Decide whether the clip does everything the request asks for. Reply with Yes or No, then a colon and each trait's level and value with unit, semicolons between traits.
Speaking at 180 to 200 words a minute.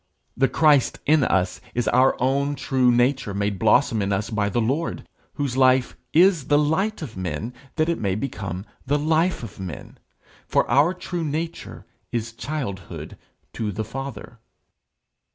No: average, 155 wpm